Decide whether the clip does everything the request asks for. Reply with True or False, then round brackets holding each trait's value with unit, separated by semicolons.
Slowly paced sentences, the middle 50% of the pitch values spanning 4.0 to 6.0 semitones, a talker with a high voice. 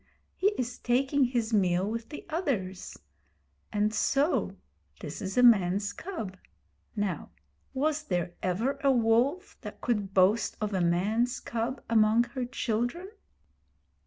True (130 wpm; 4.7 semitones; 230 Hz)